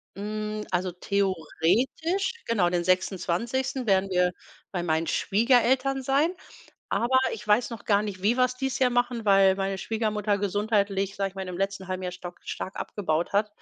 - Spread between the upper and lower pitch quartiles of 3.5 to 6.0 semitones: Yes, average, 4.1 semitones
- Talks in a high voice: Yes, high, 205 Hz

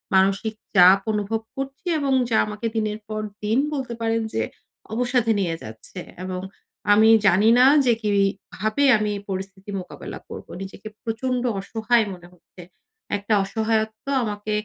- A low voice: No, high, 215 Hz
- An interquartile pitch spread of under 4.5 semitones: Yes, average, 2.7 semitones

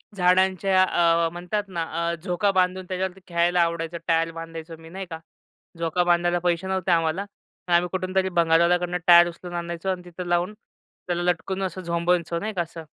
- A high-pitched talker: No, medium, 175 Hz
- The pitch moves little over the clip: Yes, narrow, 1.6 semitones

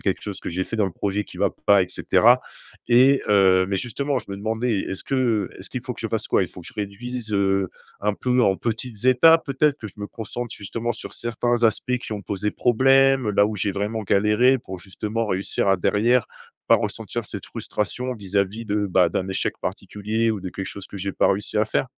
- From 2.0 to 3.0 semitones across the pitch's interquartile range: No, average, 3.5 semitones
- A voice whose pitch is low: Yes, low, 105 Hz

